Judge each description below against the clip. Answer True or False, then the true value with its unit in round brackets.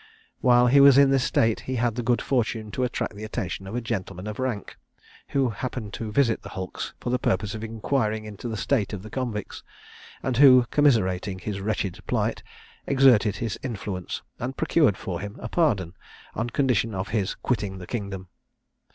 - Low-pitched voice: True (110 Hz)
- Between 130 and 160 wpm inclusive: False (185 wpm)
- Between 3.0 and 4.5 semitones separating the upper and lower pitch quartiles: True (3.8 semitones)